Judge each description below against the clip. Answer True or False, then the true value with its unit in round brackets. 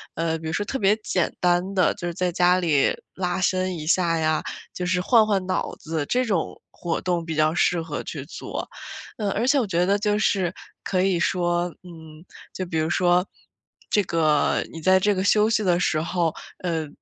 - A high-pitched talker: False (180 Hz)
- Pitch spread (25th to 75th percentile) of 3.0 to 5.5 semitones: False (2.6 semitones)